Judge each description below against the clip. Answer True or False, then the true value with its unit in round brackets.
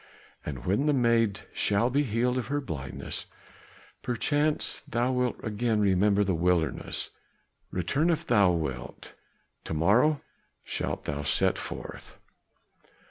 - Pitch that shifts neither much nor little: False (6.0 semitones)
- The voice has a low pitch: True (110 Hz)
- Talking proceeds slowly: True (125 wpm)